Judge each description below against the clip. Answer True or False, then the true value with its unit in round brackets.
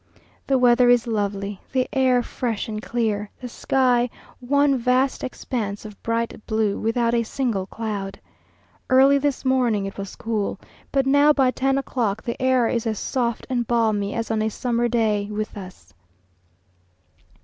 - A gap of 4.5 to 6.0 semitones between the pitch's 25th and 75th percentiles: False (3.2 semitones)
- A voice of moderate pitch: False (235 Hz)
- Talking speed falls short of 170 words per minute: True (160 wpm)